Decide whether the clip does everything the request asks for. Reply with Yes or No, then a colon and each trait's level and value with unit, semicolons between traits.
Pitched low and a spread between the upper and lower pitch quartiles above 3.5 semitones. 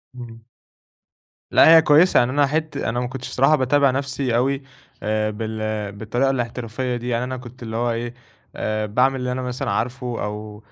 No: low, 125 Hz; average, 2.9 semitones